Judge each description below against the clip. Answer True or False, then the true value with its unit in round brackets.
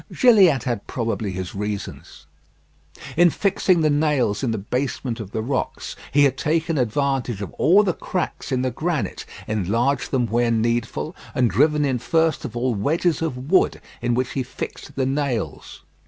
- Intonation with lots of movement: False (4.8 semitones)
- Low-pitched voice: True (130 Hz)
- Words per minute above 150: True (170 wpm)